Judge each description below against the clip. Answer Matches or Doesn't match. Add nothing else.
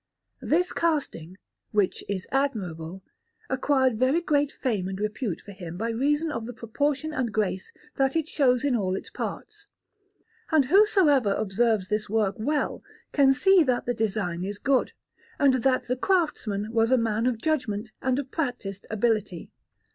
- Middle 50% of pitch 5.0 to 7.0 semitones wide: Matches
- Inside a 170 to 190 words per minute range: Doesn't match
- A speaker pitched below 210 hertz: Doesn't match